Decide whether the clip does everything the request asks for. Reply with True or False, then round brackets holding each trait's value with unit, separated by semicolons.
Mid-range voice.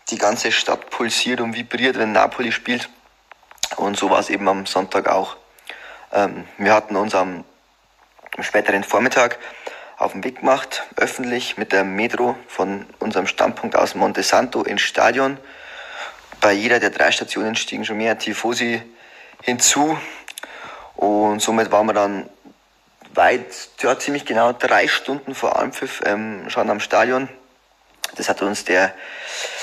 False (115 Hz)